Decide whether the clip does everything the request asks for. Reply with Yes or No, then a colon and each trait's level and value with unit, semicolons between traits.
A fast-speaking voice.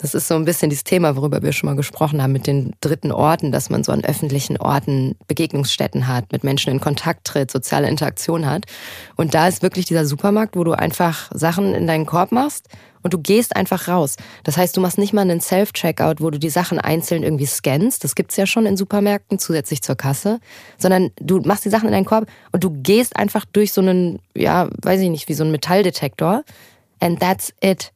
Yes: fast, 220 wpm